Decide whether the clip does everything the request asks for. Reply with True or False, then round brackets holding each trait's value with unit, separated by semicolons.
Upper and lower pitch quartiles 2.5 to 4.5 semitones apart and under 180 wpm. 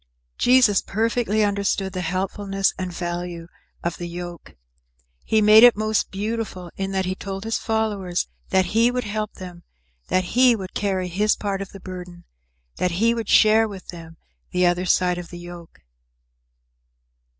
True (3.3 semitones; 160 wpm)